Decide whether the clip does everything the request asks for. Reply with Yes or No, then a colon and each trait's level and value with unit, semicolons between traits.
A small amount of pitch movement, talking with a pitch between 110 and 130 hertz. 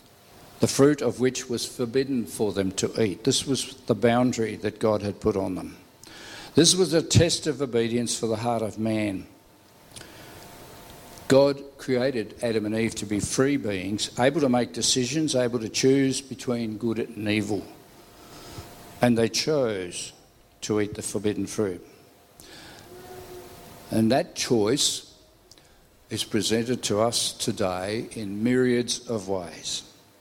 No: average, 3.1 semitones; low, 115 Hz